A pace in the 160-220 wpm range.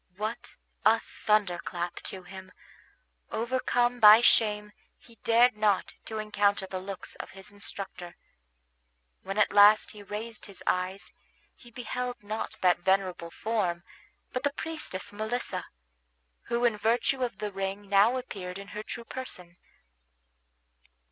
No: slow, 135 wpm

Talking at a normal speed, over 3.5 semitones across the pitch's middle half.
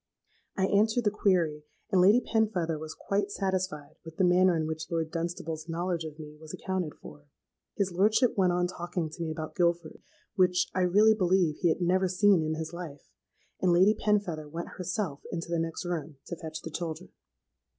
No: average, 190 wpm; average, 2.9 semitones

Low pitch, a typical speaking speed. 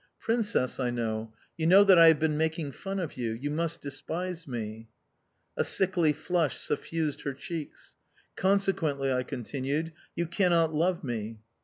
No: medium, 160 Hz; average, 155 wpm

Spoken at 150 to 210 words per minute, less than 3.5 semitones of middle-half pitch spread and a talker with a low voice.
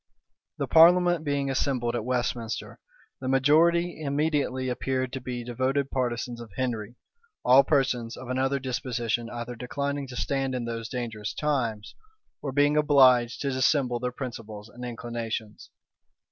No: average, 140 wpm; average, 2.8 semitones; low, 130 Hz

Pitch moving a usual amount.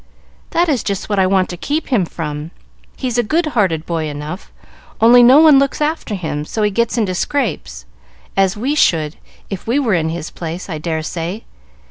No: wide, 7.1 semitones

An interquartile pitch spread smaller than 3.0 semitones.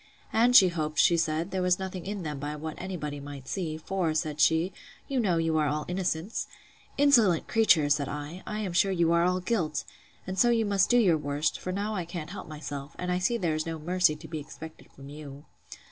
No: average, 3.7 semitones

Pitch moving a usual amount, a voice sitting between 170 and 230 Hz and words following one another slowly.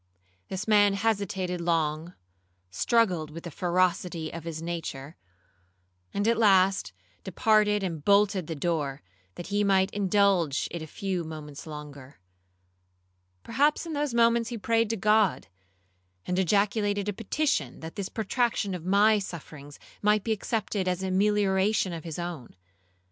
No: average, 4.0 semitones; high, 190 Hz; average, 145 wpm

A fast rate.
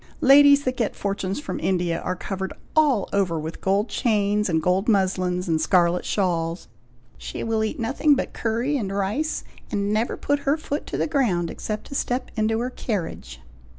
No: average, 180 wpm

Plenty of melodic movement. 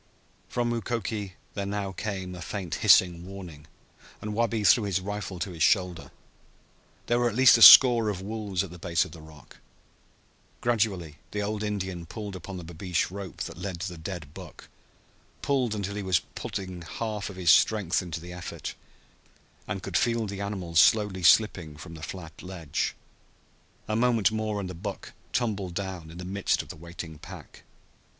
No: average, 3.3 semitones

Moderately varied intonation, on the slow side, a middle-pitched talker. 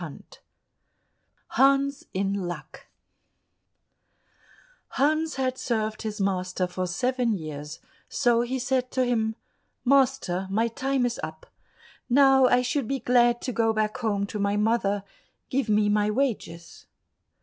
No: average, 4.3 semitones; slow, 130 wpm; high, 230 Hz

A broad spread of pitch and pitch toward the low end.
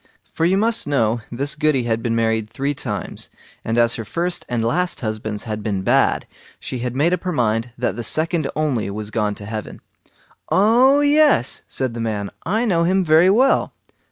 Yes: wide, 7.7 semitones; low, 125 Hz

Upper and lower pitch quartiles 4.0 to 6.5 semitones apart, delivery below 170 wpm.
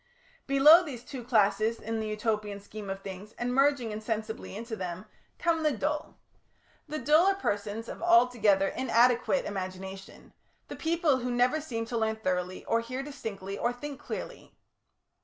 Yes: average, 4.7 semitones; average, 160 wpm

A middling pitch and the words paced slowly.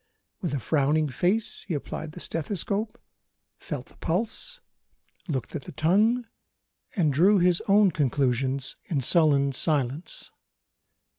Yes: medium, 160 Hz; slow, 125 wpm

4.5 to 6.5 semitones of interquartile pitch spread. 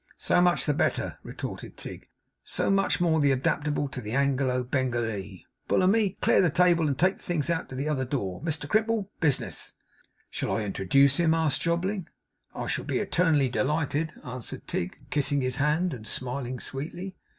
Yes: average, 5.0 semitones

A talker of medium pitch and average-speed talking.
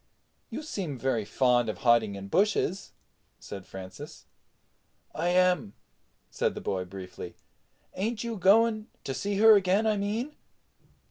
No: medium, 180 Hz; slow, 130 wpm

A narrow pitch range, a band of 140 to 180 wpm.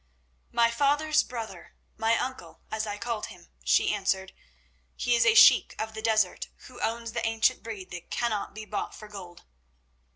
Yes: narrow, 2.2 semitones; average, 165 wpm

